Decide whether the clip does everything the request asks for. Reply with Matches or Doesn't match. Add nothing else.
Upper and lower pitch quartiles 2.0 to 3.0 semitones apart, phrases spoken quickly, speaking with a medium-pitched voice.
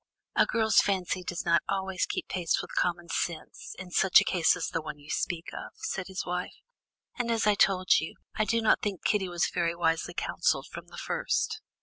Matches